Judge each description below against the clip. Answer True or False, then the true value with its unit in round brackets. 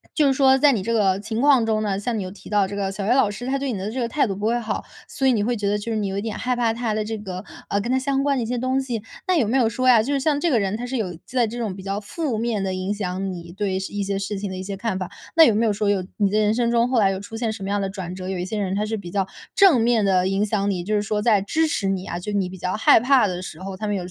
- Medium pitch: False (210 Hz)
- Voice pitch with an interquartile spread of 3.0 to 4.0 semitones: True (3.7 semitones)